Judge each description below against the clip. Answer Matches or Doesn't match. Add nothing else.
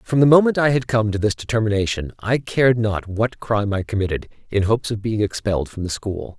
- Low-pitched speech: Matches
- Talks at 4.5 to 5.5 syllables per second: Doesn't match